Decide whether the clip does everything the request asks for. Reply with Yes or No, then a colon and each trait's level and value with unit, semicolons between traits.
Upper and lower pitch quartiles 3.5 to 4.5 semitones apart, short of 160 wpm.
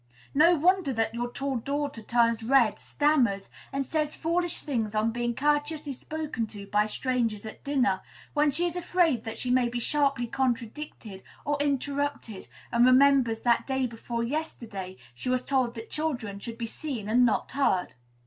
No: average, 4.2 semitones; average, 170 wpm